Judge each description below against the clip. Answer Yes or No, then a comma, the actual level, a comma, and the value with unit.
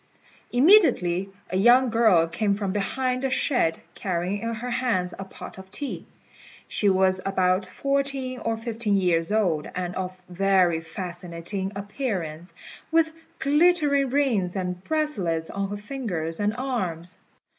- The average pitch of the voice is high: Yes, high, 200 Hz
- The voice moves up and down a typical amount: No, wide, 5.8 semitones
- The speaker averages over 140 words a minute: No, slow, 135 wpm